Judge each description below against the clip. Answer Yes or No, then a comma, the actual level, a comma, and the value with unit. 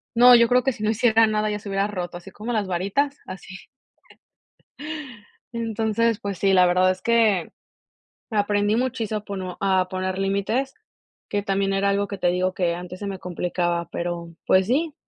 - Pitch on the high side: Yes, high, 200 Hz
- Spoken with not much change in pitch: No, average, 3.2 semitones